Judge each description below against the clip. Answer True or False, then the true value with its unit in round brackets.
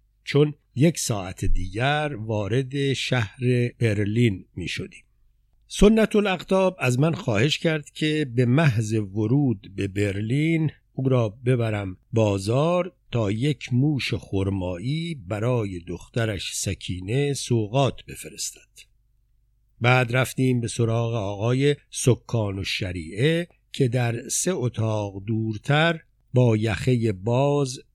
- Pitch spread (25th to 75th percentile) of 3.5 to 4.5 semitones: True (4.2 semitones)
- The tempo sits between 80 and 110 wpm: True (105 wpm)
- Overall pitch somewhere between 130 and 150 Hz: False (120 Hz)